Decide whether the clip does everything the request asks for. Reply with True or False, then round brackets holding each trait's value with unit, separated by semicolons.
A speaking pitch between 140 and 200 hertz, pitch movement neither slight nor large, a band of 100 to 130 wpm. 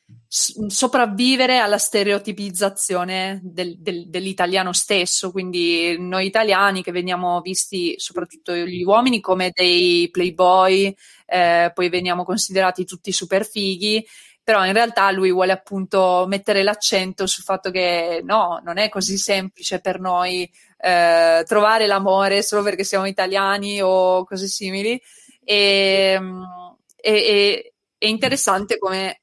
False (190 Hz; 2.2 semitones; 125 wpm)